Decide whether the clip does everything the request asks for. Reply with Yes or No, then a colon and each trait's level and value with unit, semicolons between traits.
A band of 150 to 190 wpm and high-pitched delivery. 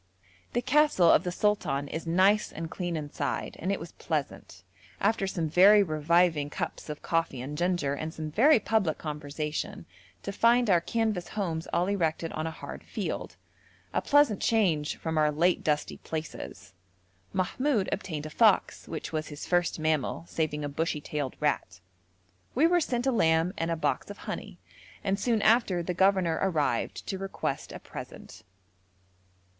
No: average, 165 wpm; medium, 170 Hz